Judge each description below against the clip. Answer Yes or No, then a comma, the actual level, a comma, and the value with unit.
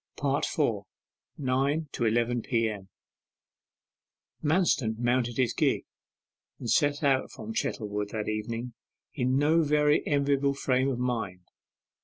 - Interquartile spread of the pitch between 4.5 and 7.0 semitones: No, average, 4.0 semitones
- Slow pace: Yes, slow, 115 wpm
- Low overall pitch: Yes, low, 125 Hz